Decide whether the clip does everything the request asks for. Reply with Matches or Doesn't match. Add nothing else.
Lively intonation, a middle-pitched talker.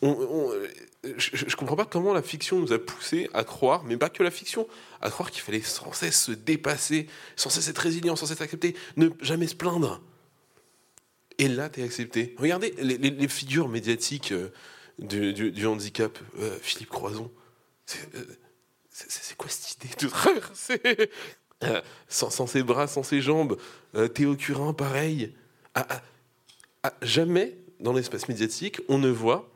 Matches